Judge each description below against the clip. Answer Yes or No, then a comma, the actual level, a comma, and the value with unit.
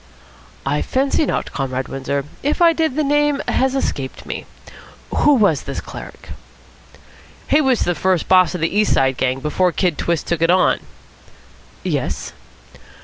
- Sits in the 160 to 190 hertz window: Yes, medium, 185 Hz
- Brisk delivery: No, average, 155 wpm